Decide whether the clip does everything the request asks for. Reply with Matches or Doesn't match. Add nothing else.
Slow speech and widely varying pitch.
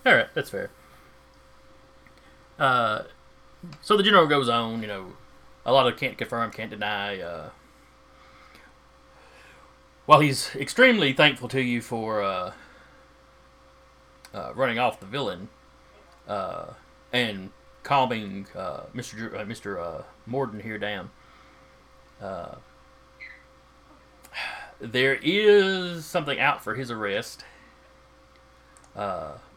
Matches